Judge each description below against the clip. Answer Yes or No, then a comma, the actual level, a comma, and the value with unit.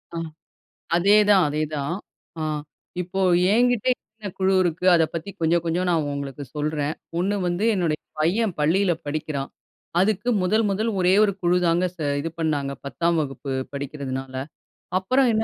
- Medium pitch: Yes, medium, 170 Hz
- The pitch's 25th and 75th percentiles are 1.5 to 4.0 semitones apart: No, average, 4.4 semitones